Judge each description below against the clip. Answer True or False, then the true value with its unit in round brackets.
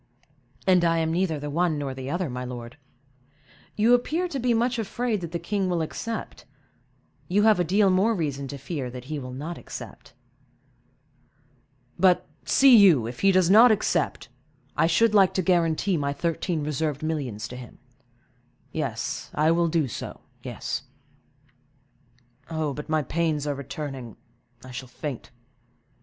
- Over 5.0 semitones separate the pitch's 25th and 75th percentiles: True (5.5 semitones)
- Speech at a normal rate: True (150 wpm)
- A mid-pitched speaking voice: True (160 Hz)